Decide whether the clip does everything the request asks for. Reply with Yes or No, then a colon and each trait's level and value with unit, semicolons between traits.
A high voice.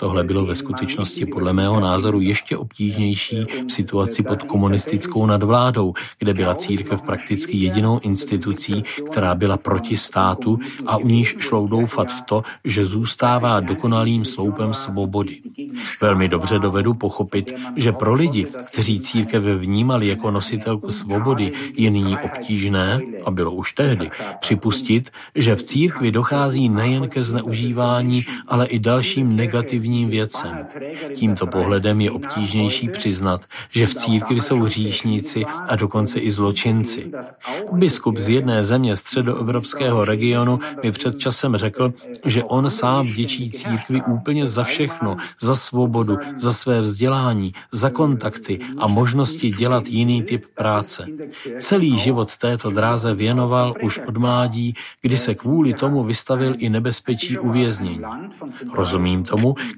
No: low, 115 Hz